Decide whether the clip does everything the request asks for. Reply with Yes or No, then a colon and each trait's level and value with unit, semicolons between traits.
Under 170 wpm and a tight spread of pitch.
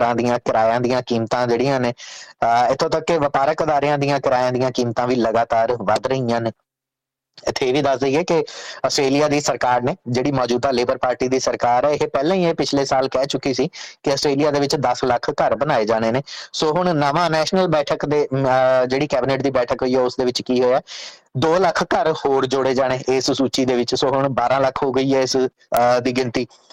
No: fast, 205 wpm; narrow, 2.2 semitones